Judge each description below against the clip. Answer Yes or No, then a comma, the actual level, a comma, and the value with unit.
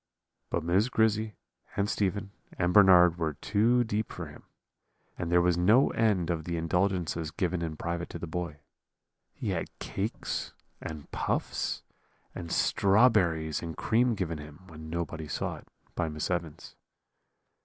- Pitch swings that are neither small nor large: Yes, average, 3.9 semitones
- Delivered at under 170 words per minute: Yes, average, 150 wpm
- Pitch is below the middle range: Yes, very low, 90 Hz